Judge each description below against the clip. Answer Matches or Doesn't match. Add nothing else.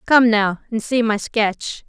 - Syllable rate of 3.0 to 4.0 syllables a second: Matches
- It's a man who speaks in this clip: Doesn't match